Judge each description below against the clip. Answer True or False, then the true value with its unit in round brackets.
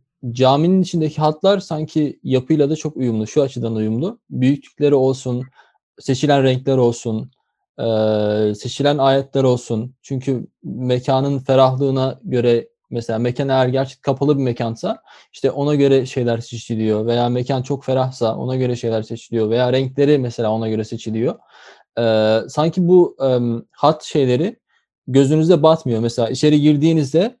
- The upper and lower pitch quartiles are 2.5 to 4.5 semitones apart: True (3.6 semitones)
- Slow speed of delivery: True (125 wpm)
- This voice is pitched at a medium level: False (130 Hz)